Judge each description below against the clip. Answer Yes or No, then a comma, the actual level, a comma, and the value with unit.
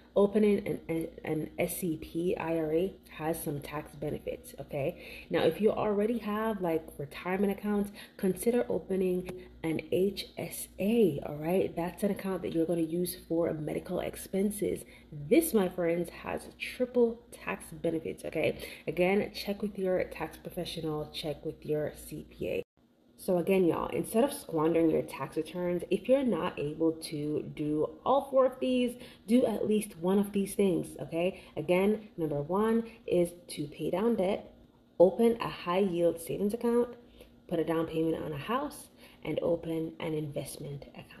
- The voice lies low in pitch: No, medium, 180 Hz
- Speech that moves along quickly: No, average, 155 wpm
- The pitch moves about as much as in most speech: Yes, average, 4.4 semitones